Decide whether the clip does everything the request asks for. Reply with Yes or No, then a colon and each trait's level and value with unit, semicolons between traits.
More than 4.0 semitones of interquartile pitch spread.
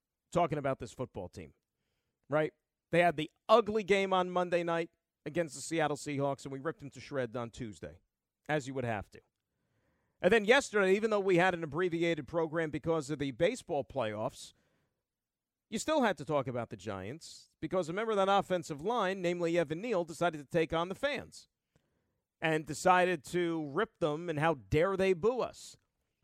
Yes: average, 4.4 semitones